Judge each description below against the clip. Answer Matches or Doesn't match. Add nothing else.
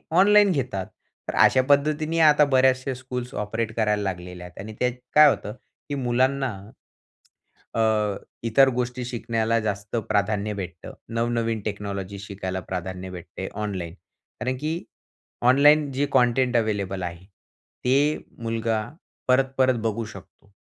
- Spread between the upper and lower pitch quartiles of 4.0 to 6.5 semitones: Matches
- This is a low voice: Matches